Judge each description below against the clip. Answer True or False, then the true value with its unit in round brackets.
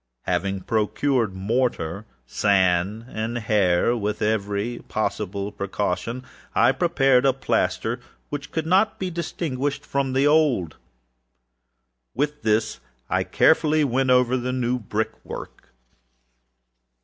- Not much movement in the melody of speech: False (4.8 semitones)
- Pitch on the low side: True (120 Hz)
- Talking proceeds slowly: True (115 wpm)